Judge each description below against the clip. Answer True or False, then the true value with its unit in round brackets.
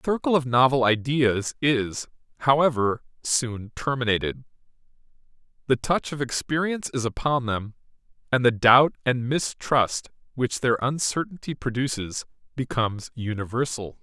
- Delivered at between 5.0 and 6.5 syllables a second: False (4.7 syllables/s)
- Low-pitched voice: True (125 Hz)